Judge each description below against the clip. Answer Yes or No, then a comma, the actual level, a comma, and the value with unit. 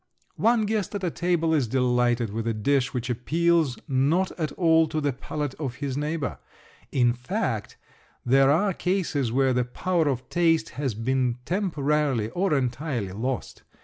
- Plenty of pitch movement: No, average, 4.8 semitones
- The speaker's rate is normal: Yes, average, 155 wpm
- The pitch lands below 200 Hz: Yes, medium, 140 Hz